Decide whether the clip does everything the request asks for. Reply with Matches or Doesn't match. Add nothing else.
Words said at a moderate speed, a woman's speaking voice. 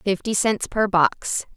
Matches